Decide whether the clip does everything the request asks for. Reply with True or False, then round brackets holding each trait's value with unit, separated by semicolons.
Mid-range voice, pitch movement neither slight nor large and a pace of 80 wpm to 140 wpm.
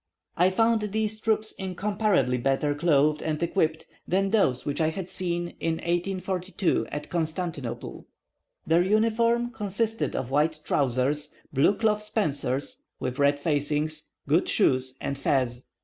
False (165 Hz; 6.0 semitones; 135 wpm)